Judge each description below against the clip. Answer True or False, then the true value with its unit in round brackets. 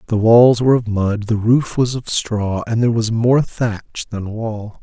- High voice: False (115 Hz)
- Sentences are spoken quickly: True (210 wpm)